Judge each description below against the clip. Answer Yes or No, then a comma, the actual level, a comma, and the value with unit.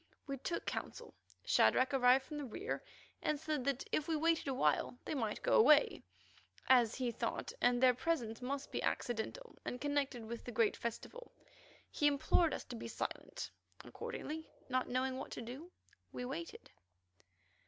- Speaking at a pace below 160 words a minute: No, average, 165 wpm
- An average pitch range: Yes, average, 3.7 semitones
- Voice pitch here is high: Yes, very high, 265 Hz